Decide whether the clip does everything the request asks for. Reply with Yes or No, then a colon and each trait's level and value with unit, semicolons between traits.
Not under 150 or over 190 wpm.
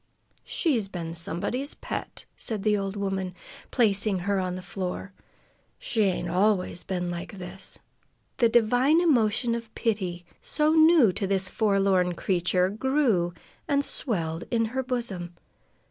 No: slow, 135 wpm